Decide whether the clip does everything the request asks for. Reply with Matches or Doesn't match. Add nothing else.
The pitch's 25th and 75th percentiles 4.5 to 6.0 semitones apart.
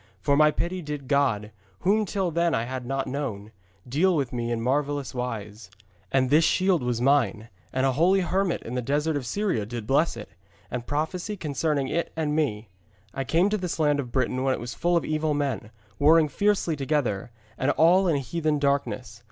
Matches